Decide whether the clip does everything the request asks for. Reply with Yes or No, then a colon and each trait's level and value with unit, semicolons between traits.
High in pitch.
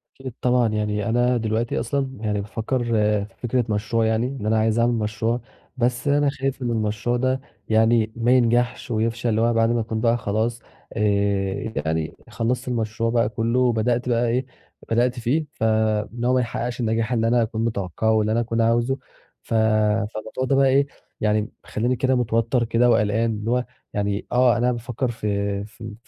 No: low, 115 Hz